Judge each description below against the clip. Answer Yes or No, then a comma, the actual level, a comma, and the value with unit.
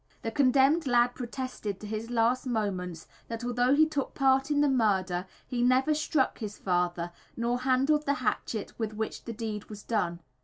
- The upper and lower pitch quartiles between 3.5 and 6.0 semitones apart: Yes, average, 4.0 semitones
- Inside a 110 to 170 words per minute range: No, average, 180 wpm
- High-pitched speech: Yes, high, 240 Hz